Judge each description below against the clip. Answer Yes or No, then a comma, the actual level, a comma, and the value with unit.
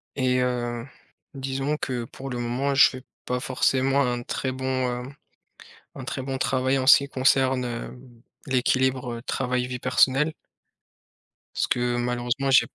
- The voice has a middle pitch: No, low, 130 Hz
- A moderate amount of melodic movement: No, narrow, 1.4 semitones